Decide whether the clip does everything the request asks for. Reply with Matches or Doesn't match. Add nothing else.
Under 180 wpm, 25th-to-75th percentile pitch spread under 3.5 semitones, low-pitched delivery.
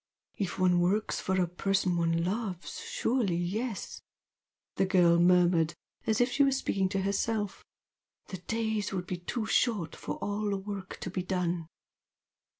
Doesn't match